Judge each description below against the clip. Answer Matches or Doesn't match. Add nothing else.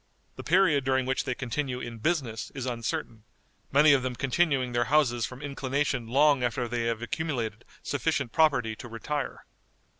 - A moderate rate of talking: Matches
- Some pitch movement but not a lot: Matches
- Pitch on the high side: Doesn't match